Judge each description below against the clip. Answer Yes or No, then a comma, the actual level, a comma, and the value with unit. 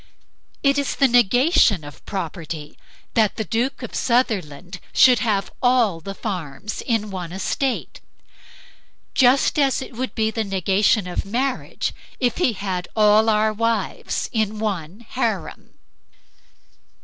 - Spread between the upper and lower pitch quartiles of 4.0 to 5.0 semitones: Yes, average, 4.3 semitones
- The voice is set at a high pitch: Yes, high, 215 Hz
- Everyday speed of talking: No, slow, 130 wpm